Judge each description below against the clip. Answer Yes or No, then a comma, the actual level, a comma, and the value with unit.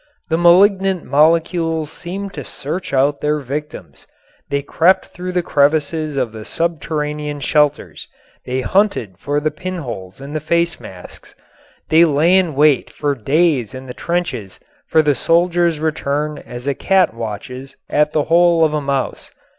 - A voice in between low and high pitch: Yes, medium, 150 Hz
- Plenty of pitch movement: No, average, 3.5 semitones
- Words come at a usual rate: Yes, average, 155 wpm